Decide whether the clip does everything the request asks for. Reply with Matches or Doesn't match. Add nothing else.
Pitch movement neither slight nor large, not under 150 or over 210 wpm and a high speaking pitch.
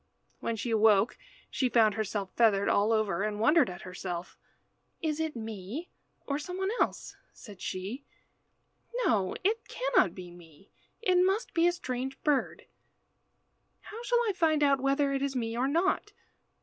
Doesn't match